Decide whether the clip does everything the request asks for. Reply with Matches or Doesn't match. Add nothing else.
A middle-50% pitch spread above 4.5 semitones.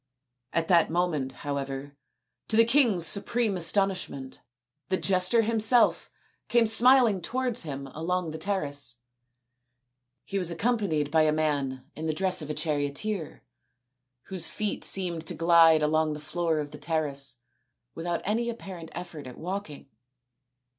Matches